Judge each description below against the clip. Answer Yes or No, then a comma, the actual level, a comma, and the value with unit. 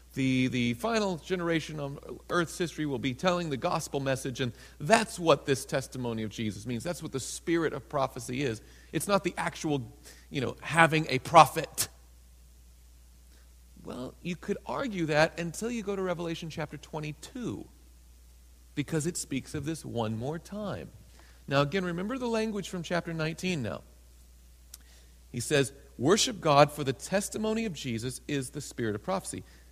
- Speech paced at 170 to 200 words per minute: No, average, 160 wpm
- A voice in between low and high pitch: Yes, medium, 145 Hz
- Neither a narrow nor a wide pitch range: No, wide, 7.5 semitones